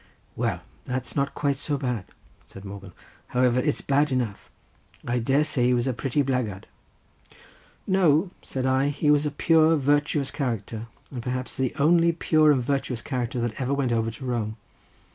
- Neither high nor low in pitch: No, low, 130 Hz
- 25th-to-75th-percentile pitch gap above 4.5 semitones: No, average, 3.3 semitones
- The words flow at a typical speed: Yes, average, 170 wpm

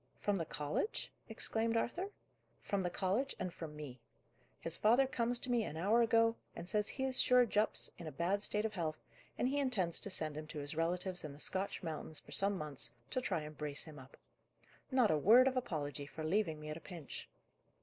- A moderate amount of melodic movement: No, wide, 6.8 semitones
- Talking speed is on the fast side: Yes, fast, 215 wpm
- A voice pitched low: No, medium, 185 Hz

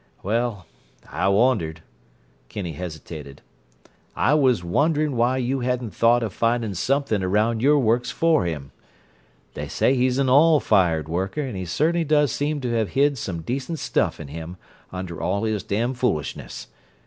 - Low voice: Yes, low, 115 Hz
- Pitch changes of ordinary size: No, wide, 6.5 semitones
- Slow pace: No, average, 150 wpm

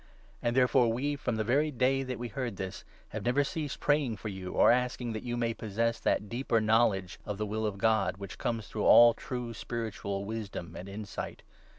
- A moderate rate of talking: No, fast, 210 wpm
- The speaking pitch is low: Yes, low, 115 Hz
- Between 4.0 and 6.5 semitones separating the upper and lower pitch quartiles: No, average, 3.2 semitones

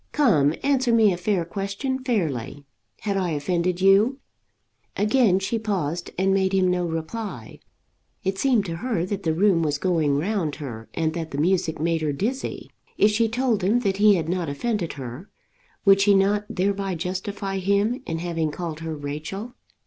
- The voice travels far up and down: No, average, 4.2 semitones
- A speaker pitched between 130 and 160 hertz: No, high, 190 Hz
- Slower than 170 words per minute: No, average, 175 wpm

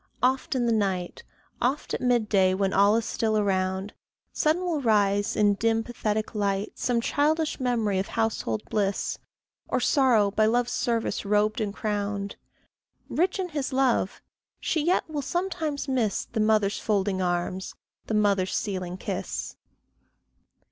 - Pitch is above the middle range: Yes, high, 215 Hz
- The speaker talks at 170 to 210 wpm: No, average, 150 wpm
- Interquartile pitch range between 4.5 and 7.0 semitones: No, average, 4.0 semitones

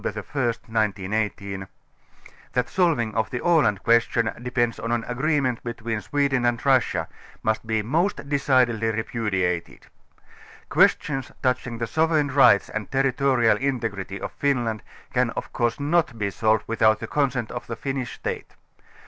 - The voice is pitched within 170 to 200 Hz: No, low, 120 Hz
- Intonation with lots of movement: No, average, 3.7 semitones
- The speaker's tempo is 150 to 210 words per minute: No, average, 140 wpm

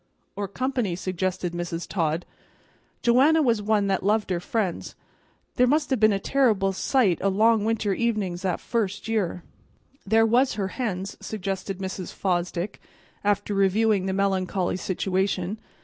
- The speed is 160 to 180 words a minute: No, average, 145 wpm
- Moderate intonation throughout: Yes, average, 3.1 semitones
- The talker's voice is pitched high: Yes, high, 200 Hz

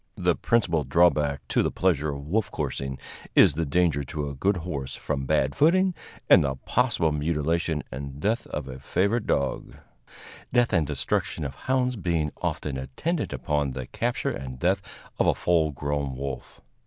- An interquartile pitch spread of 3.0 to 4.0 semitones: No, average, 4.7 semitones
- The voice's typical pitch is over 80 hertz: No, very low, 75 Hz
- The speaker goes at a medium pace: Yes, average, 165 wpm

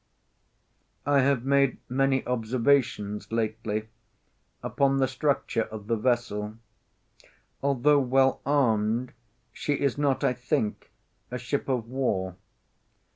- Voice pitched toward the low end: Yes, low, 125 Hz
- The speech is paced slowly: Yes, slow, 110 wpm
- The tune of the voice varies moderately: Yes, average, 3.7 semitones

